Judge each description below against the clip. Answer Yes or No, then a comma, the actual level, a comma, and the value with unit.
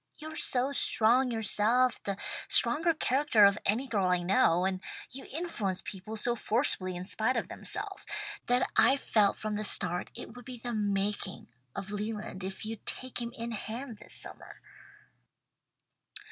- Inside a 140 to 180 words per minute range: Yes, average, 160 wpm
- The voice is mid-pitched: No, high, 220 Hz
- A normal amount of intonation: Yes, average, 3.9 semitones